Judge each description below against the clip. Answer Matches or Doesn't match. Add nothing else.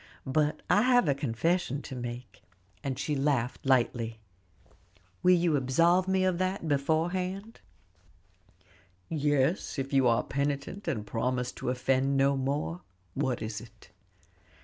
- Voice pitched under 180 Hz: Matches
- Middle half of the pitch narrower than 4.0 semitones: Doesn't match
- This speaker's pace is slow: Matches